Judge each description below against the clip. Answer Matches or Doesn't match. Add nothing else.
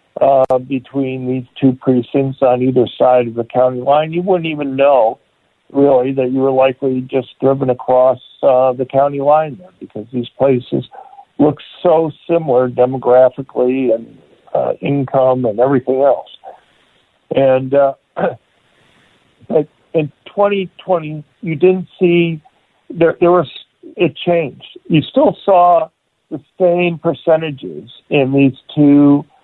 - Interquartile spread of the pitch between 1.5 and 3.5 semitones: Doesn't match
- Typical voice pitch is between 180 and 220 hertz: Doesn't match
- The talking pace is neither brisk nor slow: Doesn't match